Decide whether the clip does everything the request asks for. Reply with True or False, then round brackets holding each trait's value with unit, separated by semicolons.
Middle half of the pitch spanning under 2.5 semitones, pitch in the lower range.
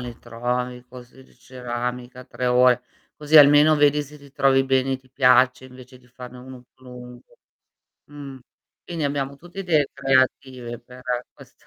True (2.0 semitones; 130 Hz)